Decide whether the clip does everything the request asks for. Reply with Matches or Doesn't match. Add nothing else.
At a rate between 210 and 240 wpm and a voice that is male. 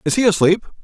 Matches